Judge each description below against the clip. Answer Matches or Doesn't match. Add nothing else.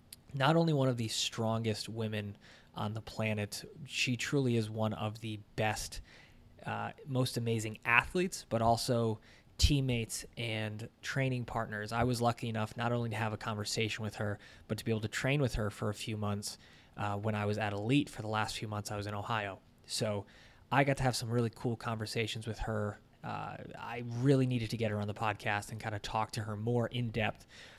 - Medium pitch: Doesn't match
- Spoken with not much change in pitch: Matches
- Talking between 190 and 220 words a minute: Matches